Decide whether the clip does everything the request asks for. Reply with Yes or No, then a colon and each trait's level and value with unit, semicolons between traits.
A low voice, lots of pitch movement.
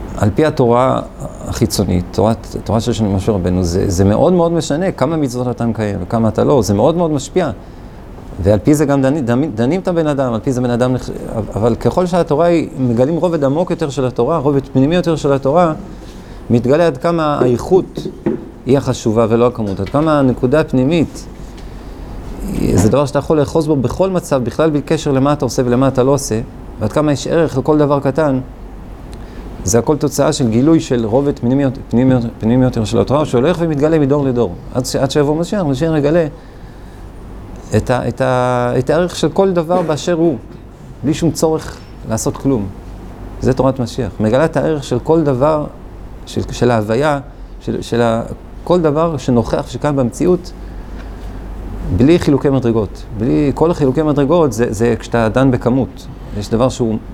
No: low, 130 Hz; average, 5.0 semitones